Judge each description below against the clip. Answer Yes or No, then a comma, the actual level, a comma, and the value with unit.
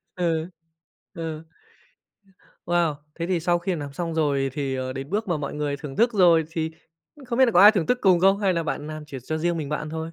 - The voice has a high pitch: No, medium, 165 Hz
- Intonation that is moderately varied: Yes, average, 3.3 semitones